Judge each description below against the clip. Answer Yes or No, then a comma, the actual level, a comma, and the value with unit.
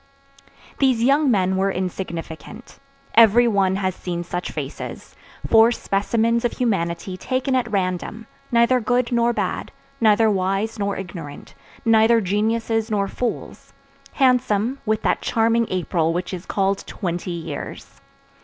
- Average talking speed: No, slow, 130 wpm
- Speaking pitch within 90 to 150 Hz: No, high, 215 Hz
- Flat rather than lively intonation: No, average, 3.8 semitones